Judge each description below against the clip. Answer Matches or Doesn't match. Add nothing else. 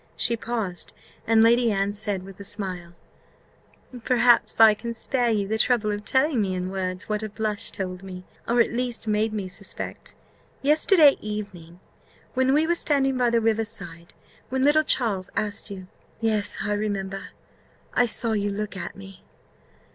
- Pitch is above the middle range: Matches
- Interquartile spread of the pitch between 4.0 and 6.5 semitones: Doesn't match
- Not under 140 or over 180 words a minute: Matches